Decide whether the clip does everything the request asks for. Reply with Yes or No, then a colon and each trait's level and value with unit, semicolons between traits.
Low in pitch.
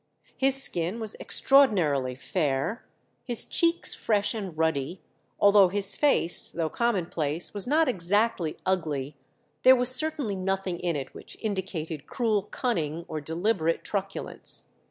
No: high, 190 Hz